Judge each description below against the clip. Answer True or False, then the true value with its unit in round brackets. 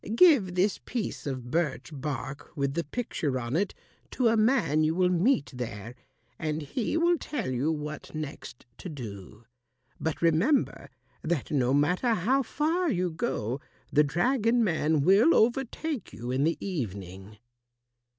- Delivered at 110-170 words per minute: True (150 wpm)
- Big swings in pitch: True (8.7 semitones)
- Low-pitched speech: False (160 Hz)